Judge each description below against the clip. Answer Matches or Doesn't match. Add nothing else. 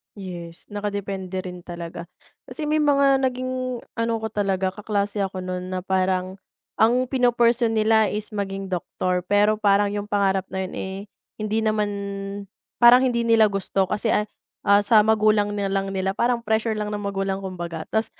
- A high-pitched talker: Matches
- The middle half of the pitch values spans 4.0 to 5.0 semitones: Doesn't match